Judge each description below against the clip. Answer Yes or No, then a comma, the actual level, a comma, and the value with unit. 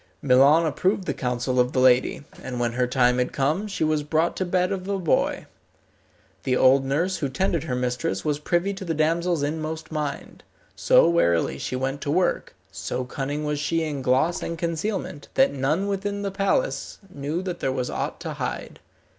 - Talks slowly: No, average, 190 wpm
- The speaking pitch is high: No, medium, 150 Hz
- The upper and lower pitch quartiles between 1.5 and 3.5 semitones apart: No, average, 5.1 semitones